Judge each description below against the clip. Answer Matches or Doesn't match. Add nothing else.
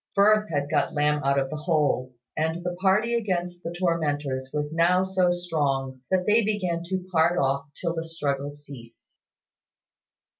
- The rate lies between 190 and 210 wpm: Doesn't match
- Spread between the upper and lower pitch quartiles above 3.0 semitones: Matches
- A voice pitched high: Doesn't match